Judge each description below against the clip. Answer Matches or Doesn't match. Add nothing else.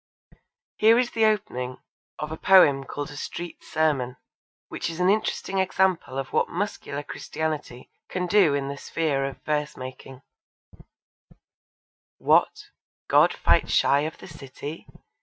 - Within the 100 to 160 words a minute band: Matches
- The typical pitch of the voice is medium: Matches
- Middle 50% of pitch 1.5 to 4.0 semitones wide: Doesn't match